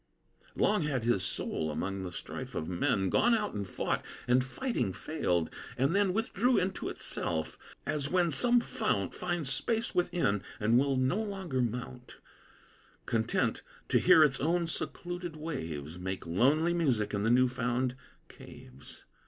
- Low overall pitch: Yes, low, 130 Hz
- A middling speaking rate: Yes, average, 150 wpm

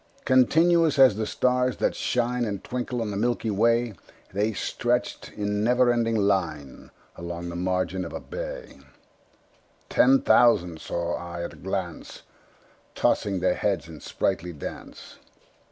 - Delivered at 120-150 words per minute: Yes, average, 140 wpm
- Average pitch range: No, wide, 5.7 semitones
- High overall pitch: No, low, 105 Hz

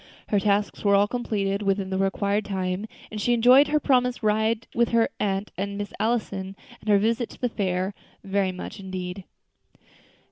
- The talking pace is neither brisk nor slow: Yes, average, 175 wpm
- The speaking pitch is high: Yes, high, 205 Hz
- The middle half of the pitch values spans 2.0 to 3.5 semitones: Yes, average, 2.8 semitones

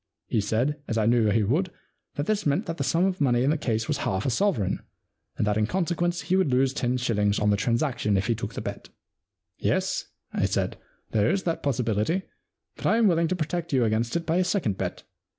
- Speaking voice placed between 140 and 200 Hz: No, low, 130 Hz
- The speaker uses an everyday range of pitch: No, wide, 7.6 semitones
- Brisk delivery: Yes, fast, 240 wpm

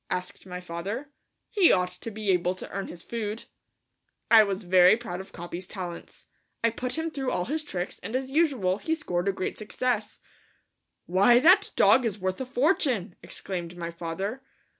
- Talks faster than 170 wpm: Yes, average, 180 wpm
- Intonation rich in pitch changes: Yes, wide, 5.9 semitones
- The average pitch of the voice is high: Yes, high, 200 Hz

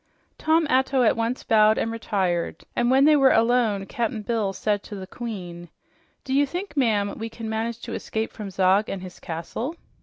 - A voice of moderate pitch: No, high, 225 Hz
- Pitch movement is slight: No, average, 3.7 semitones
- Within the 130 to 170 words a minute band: No, average, 190 wpm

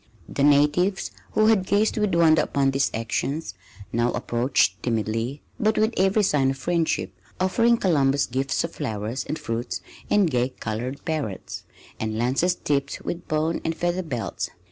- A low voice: No, medium, 145 Hz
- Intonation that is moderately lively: No, wide, 6.3 semitones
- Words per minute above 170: No, average, 155 wpm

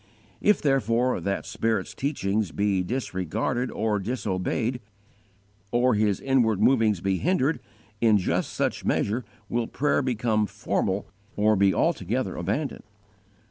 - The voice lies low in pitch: Yes, low, 110 Hz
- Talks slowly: Yes, slow, 125 wpm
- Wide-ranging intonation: No, average, 4.3 semitones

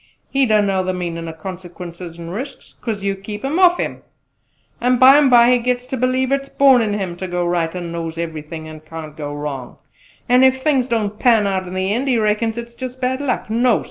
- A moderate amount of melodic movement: No, wide, 6.5 semitones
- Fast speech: Yes, fast, 220 wpm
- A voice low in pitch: No, high, 210 Hz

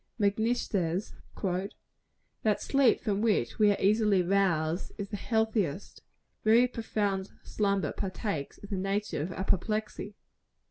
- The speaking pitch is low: No, high, 200 Hz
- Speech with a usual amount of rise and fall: No, narrow, 2.3 semitones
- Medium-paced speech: No, slow, 125 wpm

